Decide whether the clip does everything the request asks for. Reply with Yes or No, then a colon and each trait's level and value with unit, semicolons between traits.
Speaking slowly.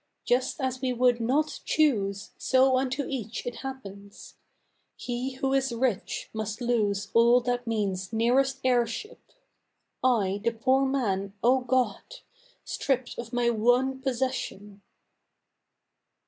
Yes: slow, 120 wpm